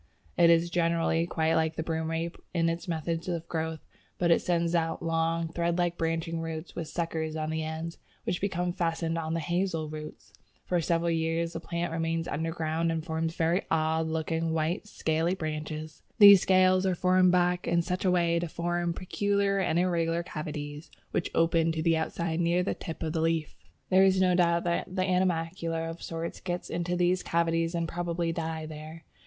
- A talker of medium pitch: Yes, medium, 165 Hz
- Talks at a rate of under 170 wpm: No, average, 185 wpm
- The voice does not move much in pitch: Yes, narrow, 1.2 semitones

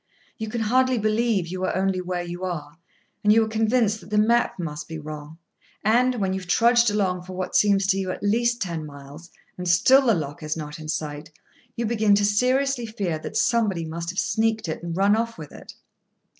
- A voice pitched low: No, high, 195 Hz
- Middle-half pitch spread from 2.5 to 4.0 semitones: No, average, 4.9 semitones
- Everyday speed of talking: No, fast, 215 wpm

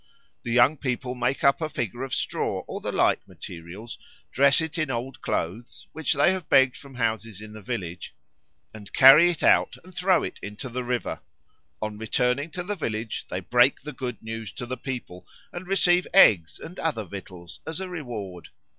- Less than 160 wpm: No, average, 190 wpm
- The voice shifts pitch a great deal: Yes, wide, 5.8 semitones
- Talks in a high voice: No, low, 125 Hz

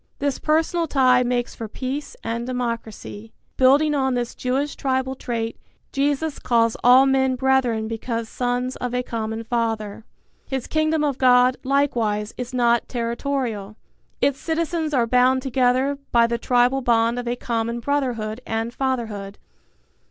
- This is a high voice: Yes, very high, 250 Hz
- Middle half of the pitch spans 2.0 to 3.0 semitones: Yes, narrow, 2.5 semitones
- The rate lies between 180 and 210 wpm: No, average, 145 wpm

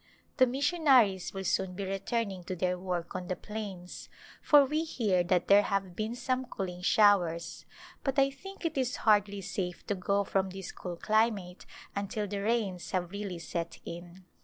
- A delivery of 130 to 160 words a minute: No, average, 180 wpm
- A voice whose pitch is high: Yes, high, 195 Hz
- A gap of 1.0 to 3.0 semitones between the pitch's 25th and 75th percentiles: No, average, 4.0 semitones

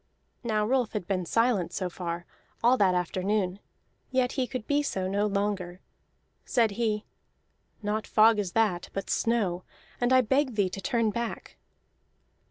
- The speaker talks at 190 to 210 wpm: No, average, 155 wpm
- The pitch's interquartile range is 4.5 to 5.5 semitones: No, average, 4.0 semitones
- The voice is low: No, high, 210 Hz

